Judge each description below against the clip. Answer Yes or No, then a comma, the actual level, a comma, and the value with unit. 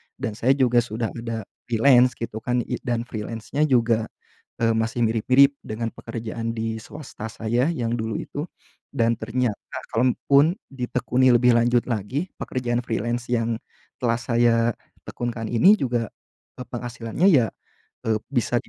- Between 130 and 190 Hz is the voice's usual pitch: No, low, 120 Hz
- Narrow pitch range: Yes, narrow, 1.7 semitones